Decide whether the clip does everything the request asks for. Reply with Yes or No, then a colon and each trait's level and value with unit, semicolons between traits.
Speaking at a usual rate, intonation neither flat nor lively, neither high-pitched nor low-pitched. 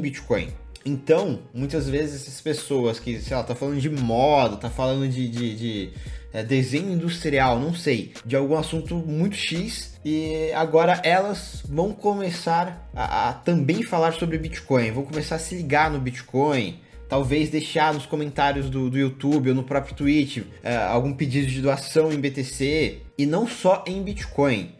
Yes: average, 165 wpm; average, 3.3 semitones; medium, 145 Hz